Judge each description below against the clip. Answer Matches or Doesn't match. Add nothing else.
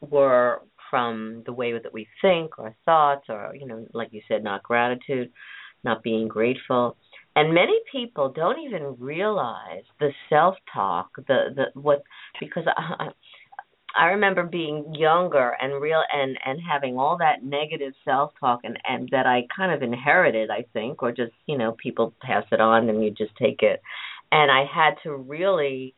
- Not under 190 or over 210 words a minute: Doesn't match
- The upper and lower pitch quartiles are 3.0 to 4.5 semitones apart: Doesn't match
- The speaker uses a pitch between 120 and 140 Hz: Matches